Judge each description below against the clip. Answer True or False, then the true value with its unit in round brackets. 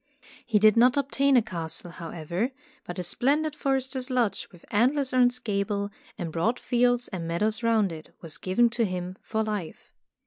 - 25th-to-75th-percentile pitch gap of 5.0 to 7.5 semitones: True (5.5 semitones)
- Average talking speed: True (175 wpm)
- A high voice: True (220 Hz)